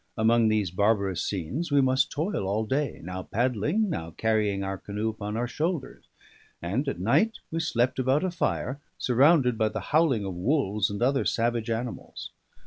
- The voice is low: Yes, low, 115 Hz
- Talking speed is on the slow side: No, average, 170 wpm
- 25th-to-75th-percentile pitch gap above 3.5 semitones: Yes, average, 5.1 semitones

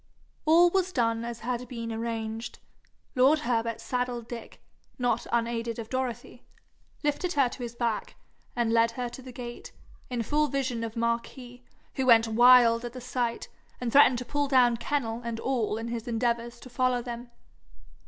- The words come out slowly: No, average, 170 wpm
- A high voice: Yes, high, 240 Hz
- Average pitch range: No, narrow, 1.7 semitones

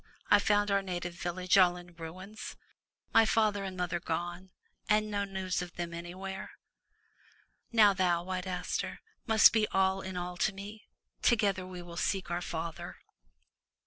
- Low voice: No, medium, 185 Hz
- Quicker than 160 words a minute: No, average, 155 wpm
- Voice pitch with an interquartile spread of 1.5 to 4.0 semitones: Yes, narrow, 2.4 semitones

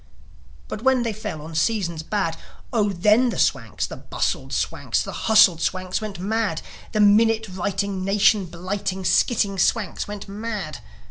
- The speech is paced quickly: No, average, 150 wpm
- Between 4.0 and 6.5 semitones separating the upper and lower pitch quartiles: No, average, 2.8 semitones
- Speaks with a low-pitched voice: No, high, 200 Hz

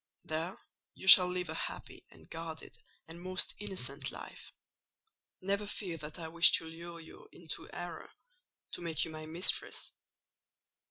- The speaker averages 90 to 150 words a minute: Yes, average, 145 wpm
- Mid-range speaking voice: Yes, medium, 170 Hz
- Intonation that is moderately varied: No, narrow, 2.3 semitones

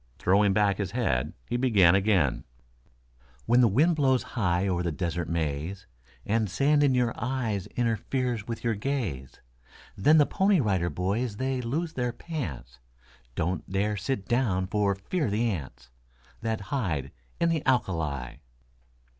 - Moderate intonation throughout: No, wide, 6.1 semitones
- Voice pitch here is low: Yes, low, 105 Hz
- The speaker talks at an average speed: Yes, average, 155 wpm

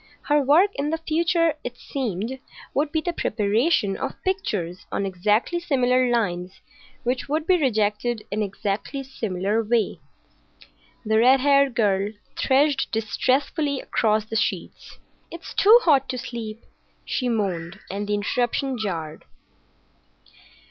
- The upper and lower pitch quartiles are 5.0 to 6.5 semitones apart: Yes, average, 5.3 semitones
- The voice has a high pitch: Yes, high, 240 Hz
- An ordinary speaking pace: No, slow, 130 wpm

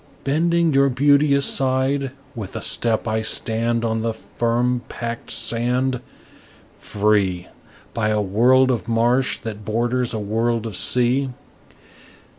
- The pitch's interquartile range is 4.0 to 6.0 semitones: No, average, 2.8 semitones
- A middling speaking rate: No, slow, 125 wpm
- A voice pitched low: Yes, low, 120 Hz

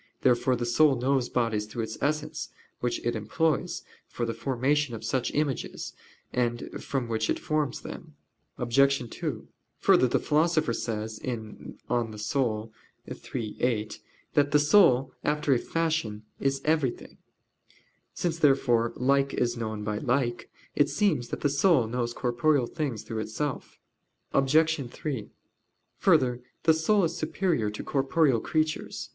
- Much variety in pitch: No, average, 4.2 semitones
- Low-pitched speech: Yes, low, 130 Hz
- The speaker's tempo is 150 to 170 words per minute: No, average, 140 wpm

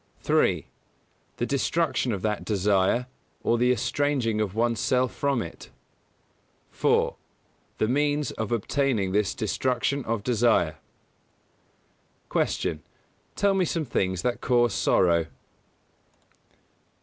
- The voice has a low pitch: Yes, low, 120 Hz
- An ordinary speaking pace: No, slow, 115 wpm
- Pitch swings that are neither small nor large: Yes, average, 4.2 semitones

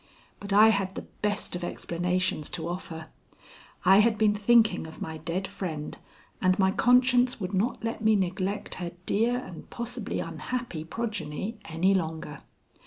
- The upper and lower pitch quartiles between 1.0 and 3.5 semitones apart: No, average, 4.4 semitones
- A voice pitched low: No, high, 190 Hz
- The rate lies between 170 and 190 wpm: No, average, 155 wpm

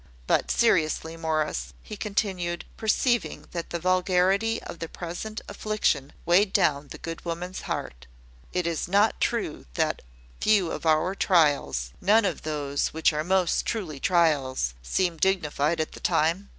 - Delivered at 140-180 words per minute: Yes, average, 150 wpm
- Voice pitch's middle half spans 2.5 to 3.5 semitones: No, average, 3.9 semitones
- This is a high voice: No, medium, 175 Hz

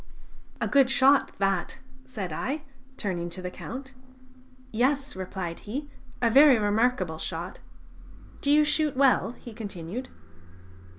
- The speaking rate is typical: No, slow, 125 wpm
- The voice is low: No, high, 235 Hz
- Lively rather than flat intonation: Yes, wide, 6.5 semitones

